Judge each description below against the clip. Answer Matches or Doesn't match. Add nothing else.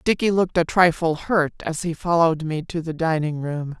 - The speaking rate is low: Doesn't match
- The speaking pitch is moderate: Matches